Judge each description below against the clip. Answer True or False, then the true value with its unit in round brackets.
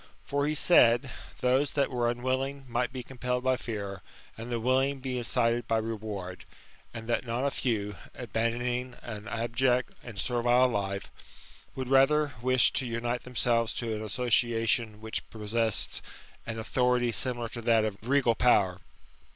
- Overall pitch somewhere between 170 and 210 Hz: False (120 Hz)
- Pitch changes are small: True (2.1 semitones)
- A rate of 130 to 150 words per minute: False (160 wpm)